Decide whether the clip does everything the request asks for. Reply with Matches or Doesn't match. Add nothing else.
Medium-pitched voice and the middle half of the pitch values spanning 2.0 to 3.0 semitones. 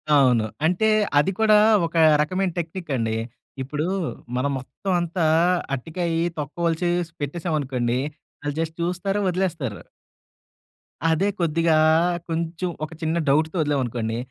Doesn't match